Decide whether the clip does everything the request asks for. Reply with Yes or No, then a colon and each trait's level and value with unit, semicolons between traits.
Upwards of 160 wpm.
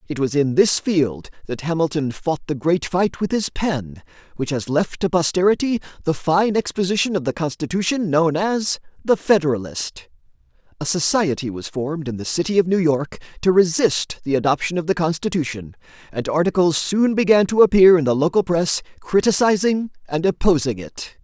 Yes: average, 170 wpm